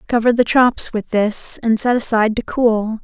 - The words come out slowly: No, average, 200 wpm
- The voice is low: No, high, 225 Hz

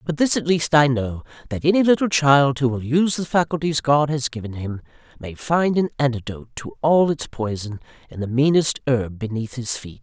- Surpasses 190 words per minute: Yes, fast, 205 wpm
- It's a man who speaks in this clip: Yes, male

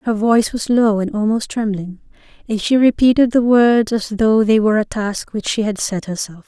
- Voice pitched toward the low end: No, high, 215 Hz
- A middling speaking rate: No, fast, 215 wpm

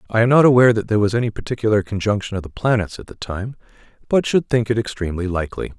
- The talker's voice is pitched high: No, low, 110 Hz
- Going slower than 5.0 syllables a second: No, 7.3 syllables/s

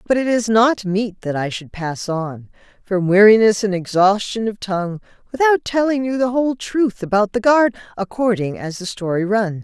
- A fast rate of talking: No, average, 185 wpm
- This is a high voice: Yes, high, 210 Hz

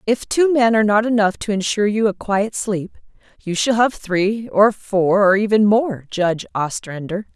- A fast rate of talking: No, average, 190 wpm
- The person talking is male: No, female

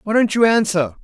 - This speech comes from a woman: Yes, female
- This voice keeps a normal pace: No, fast, 230 wpm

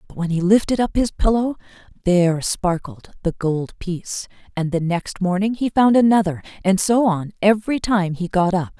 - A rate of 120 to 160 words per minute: No, average, 185 wpm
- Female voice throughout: Yes, female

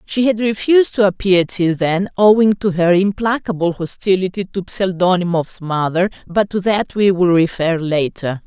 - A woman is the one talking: Yes, female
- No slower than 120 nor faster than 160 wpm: Yes, average, 155 wpm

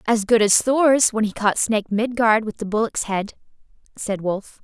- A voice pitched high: Yes, high, 215 Hz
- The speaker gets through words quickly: No, average, 195 wpm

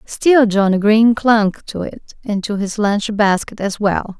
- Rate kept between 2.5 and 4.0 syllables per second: Yes, 3.9 syllables/s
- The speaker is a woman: Yes, female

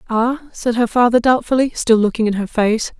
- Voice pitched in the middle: No, high, 235 Hz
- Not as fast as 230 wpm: Yes, average, 200 wpm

